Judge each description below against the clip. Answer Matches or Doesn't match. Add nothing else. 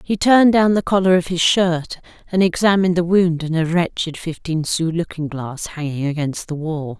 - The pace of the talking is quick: Doesn't match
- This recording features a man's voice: Doesn't match